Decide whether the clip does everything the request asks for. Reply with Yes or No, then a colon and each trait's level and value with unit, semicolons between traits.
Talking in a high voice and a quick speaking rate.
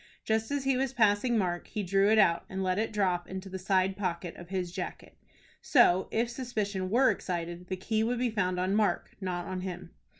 Yes: high, 195 Hz; fast, 210 wpm